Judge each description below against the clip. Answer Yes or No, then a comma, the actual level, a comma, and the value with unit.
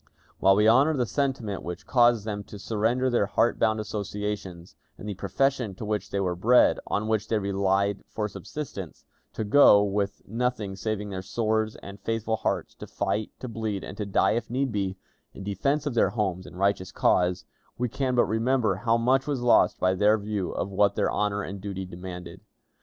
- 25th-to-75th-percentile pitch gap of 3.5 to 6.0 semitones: No, average, 3.0 semitones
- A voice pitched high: No, low, 105 Hz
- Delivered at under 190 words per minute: No, average, 195 wpm